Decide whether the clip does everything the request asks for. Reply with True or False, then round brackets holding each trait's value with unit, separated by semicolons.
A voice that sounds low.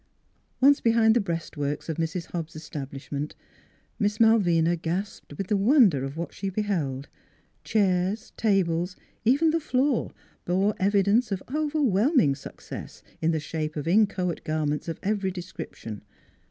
False (185 Hz)